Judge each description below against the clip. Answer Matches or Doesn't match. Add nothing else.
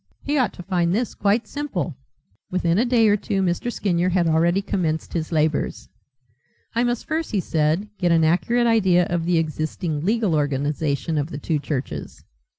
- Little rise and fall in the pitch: Doesn't match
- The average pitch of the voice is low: Doesn't match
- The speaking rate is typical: Matches